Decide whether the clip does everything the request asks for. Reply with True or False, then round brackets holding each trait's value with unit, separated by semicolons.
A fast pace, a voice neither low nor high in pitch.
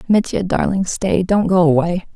False (165 wpm; 180 Hz)